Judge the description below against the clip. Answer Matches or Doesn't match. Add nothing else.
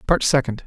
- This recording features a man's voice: Matches